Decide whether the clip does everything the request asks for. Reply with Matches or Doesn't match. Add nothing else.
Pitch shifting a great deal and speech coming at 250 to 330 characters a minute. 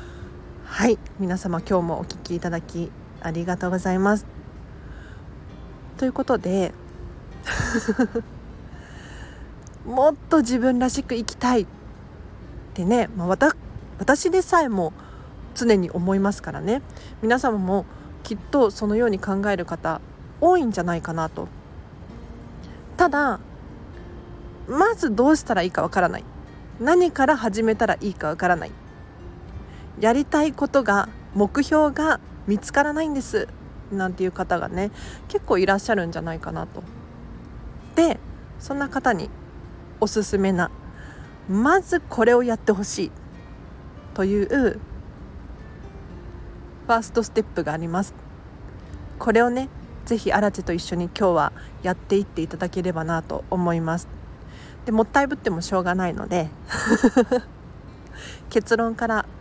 Matches